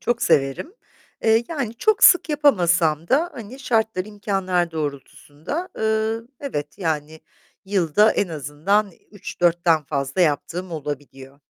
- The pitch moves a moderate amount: No, wide, 6.5 semitones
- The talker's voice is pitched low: No, medium, 185 Hz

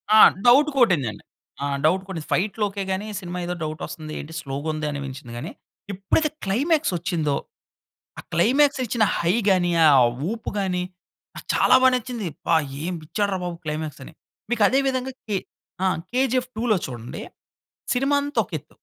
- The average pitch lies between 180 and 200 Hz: Yes, high, 190 Hz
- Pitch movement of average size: No, wide, 7.8 semitones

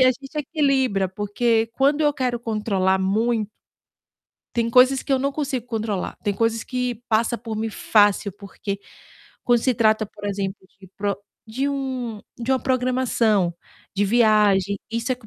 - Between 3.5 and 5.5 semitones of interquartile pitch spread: Yes, average, 3.8 semitones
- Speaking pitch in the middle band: No, high, 230 Hz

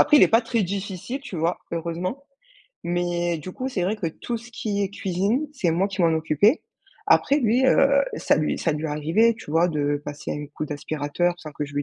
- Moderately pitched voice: Yes, medium, 175 Hz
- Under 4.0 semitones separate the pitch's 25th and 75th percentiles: No, wide, 5.9 semitones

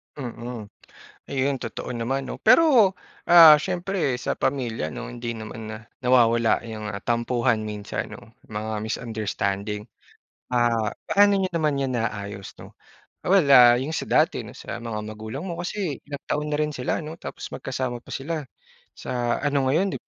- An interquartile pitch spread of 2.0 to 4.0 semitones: No, average, 5.1 semitones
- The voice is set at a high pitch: No, low, 125 Hz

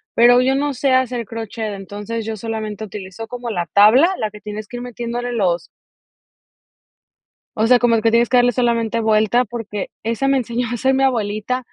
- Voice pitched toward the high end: Yes, high, 230 Hz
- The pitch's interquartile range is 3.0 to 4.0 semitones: No, narrow, 2.5 semitones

